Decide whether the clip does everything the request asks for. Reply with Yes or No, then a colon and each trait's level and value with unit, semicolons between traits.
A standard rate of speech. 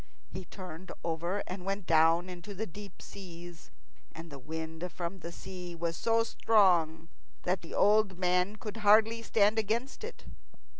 Yes: average, 155 wpm